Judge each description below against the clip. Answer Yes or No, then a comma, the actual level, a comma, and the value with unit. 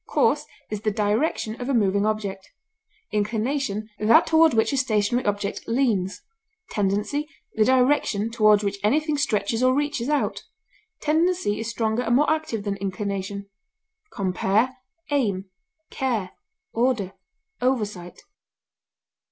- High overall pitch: Yes, high, 220 Hz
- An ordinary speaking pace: No, slow, 120 wpm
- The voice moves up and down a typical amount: Yes, average, 4.4 semitones